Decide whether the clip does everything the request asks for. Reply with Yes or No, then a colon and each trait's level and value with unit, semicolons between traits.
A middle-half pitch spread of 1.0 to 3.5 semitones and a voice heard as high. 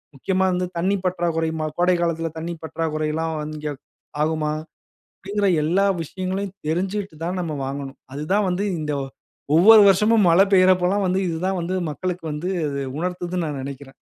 No: average, 3.1 semitones; medium, 175 Hz